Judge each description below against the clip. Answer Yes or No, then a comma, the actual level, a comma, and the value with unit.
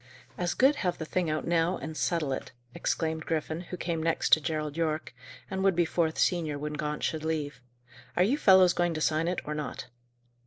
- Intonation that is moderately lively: No, narrow, 2.3 semitones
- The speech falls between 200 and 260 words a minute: Yes, fast, 205 wpm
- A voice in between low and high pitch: Yes, medium, 160 Hz